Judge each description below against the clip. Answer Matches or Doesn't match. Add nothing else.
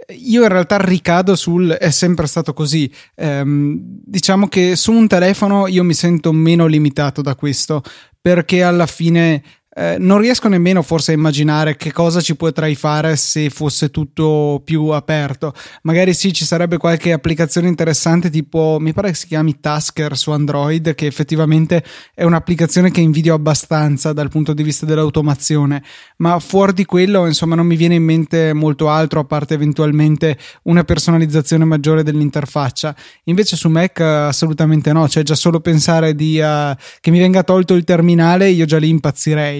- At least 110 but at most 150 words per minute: Doesn't match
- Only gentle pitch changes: Matches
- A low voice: Doesn't match